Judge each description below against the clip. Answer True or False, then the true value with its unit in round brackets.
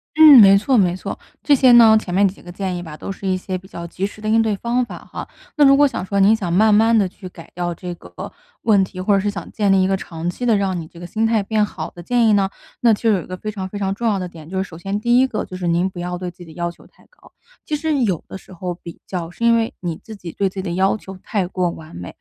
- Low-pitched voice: False (195 Hz)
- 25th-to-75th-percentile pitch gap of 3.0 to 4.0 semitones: True (3.6 semitones)